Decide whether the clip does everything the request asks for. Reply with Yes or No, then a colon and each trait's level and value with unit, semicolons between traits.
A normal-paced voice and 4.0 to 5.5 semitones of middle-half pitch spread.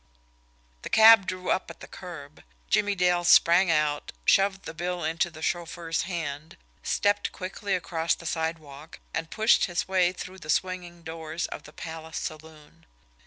No: average, 160 wpm; narrow, 2.5 semitones